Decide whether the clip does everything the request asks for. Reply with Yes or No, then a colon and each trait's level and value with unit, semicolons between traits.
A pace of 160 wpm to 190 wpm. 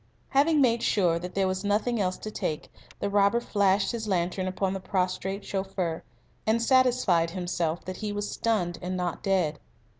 Yes: average, 175 wpm